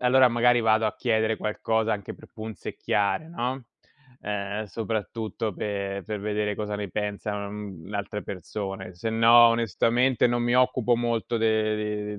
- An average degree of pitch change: No, narrow, 2.1 semitones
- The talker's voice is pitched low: Yes, low, 110 Hz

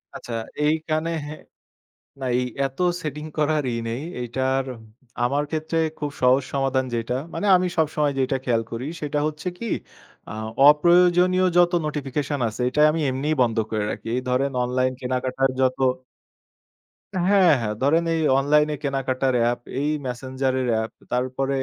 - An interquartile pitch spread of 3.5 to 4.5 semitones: No, average, 3.1 semitones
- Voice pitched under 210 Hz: Yes, low, 135 Hz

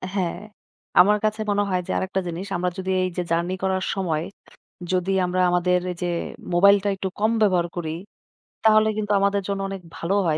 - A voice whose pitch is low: No, high, 190 Hz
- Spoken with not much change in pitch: Yes, narrow, 2.0 semitones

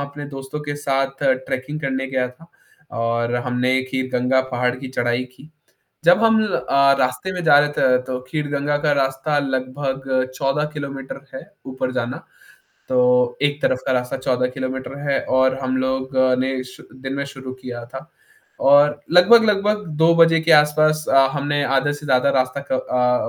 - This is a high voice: No, low, 135 Hz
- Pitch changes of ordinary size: No, narrow, 2.2 semitones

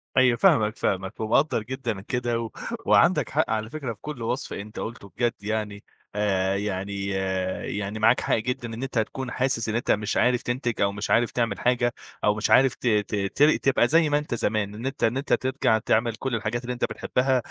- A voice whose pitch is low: Yes, low, 115 Hz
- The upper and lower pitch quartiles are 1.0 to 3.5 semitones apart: Yes, average, 3.1 semitones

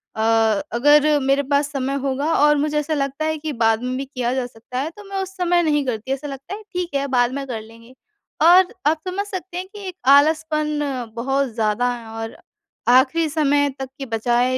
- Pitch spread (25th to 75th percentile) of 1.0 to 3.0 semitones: No, average, 4.0 semitones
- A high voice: Yes, very high, 280 Hz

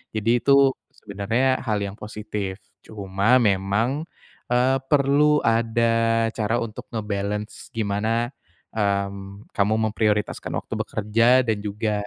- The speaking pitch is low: Yes, low, 110 Hz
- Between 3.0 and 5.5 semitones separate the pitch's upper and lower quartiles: No, narrow, 2.4 semitones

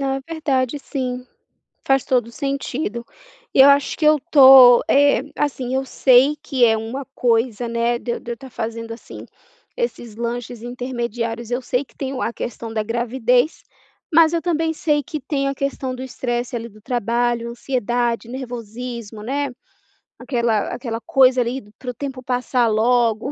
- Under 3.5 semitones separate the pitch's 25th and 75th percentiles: Yes, narrow, 2.5 semitones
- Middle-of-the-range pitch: No, high, 245 Hz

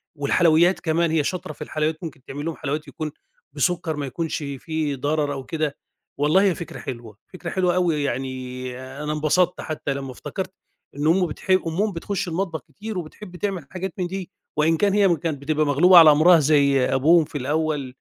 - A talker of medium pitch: Yes, medium, 155 Hz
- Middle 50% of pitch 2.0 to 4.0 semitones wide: Yes, average, 3.5 semitones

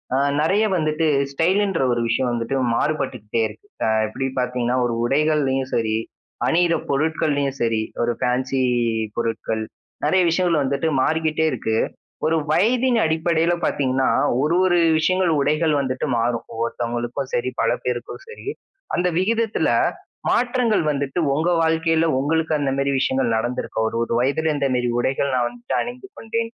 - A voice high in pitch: No, medium, 145 Hz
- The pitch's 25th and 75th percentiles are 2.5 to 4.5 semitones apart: No, average, 5.0 semitones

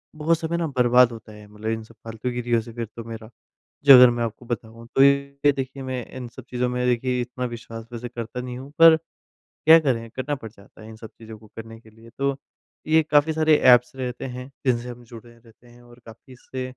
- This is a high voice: No, low, 125 Hz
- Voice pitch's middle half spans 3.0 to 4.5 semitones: No, narrow, 2.4 semitones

